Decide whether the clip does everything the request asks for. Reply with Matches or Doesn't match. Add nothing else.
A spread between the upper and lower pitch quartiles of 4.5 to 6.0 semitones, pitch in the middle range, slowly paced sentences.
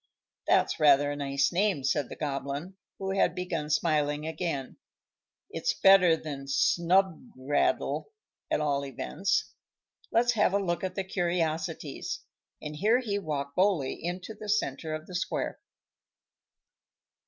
Matches